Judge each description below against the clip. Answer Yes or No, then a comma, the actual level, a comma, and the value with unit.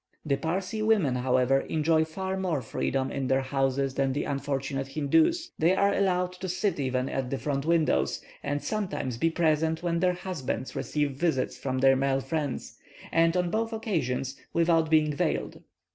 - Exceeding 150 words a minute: Yes, average, 170 wpm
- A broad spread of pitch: No, average, 4.7 semitones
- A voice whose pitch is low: No, medium, 155 Hz